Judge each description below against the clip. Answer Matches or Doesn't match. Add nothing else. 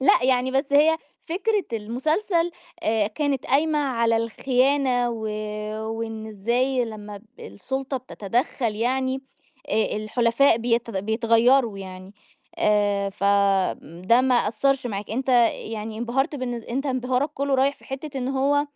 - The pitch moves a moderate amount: Matches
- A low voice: Doesn't match